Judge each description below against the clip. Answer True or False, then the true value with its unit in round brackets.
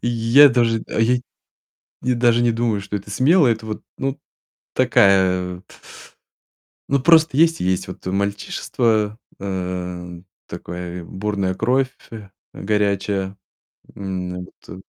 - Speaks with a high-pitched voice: False (105 Hz)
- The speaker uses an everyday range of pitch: True (4.3 semitones)